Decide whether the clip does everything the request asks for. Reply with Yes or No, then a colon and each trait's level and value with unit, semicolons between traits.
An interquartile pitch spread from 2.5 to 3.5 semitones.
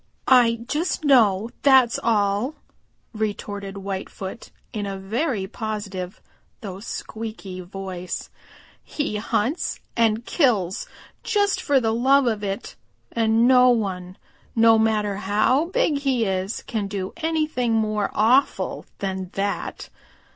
No: average, 4.1 semitones